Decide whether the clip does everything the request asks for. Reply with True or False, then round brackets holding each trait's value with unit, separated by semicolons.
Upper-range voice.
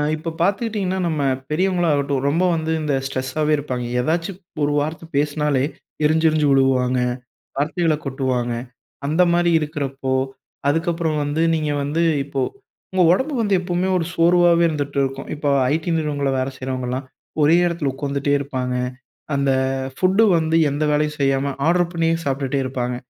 False (150 Hz)